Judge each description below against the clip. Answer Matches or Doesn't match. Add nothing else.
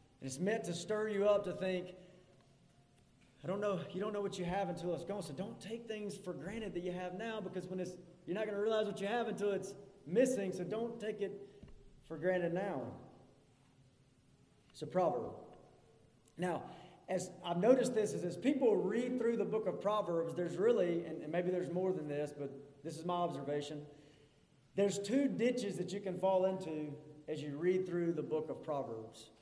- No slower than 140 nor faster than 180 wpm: Doesn't match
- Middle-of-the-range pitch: Matches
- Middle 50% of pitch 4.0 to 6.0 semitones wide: Matches